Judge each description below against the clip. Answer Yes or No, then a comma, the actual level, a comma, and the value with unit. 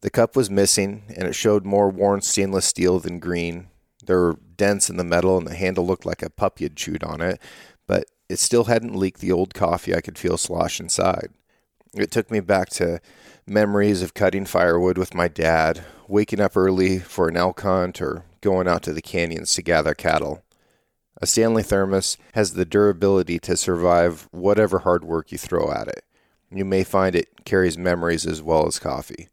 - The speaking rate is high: No, average, 195 wpm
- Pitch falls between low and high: No, very low, 95 Hz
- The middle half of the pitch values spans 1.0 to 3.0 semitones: Yes, narrow, 2.5 semitones